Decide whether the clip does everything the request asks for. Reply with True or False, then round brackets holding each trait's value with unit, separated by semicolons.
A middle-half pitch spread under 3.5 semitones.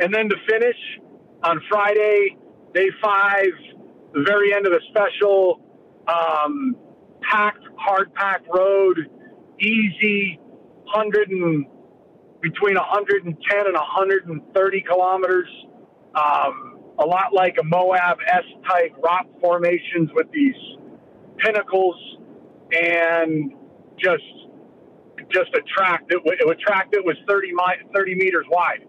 True (3.0 semitones)